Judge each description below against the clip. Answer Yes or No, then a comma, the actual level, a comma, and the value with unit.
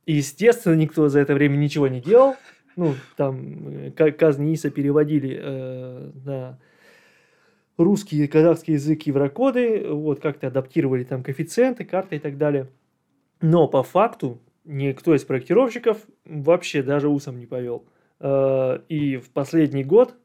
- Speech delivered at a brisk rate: No, average, 135 wpm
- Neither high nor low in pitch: Yes, medium, 150 Hz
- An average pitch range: Yes, average, 3.3 semitones